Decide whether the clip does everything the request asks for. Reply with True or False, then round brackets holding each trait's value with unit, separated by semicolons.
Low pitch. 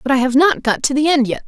False (270 Hz)